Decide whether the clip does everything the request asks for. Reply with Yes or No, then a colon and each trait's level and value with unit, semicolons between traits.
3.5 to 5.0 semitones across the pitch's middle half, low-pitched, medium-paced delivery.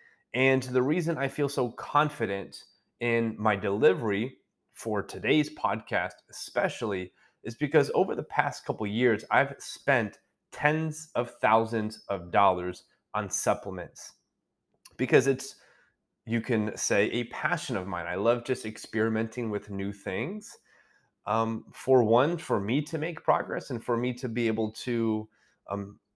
Yes: average, 3.8 semitones; low, 115 Hz; average, 145 wpm